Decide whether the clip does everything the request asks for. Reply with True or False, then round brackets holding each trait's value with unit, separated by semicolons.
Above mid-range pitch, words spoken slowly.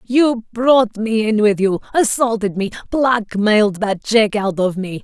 False (215 Hz; 165 wpm)